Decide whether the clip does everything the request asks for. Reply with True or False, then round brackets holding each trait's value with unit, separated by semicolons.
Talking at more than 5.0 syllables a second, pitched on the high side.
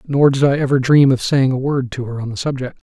False (5.9 syllables/s; 135 Hz)